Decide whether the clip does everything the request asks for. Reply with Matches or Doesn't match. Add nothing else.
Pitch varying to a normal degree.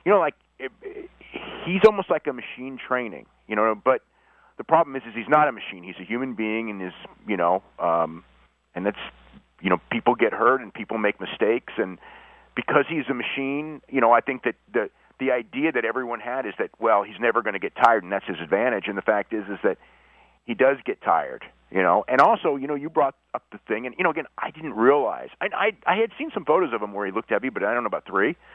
Doesn't match